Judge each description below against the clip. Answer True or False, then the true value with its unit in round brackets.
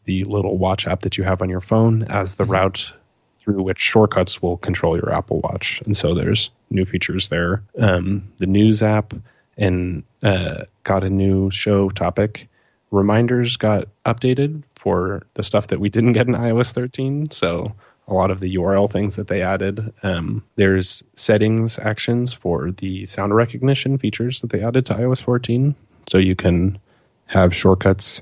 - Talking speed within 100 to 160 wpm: False (170 wpm)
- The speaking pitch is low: True (100 Hz)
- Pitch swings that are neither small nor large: True (3.3 semitones)